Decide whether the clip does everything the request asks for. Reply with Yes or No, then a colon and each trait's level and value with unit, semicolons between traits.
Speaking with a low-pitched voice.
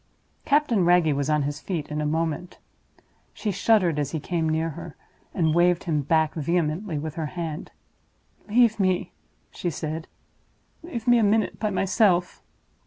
No: medium, 170 Hz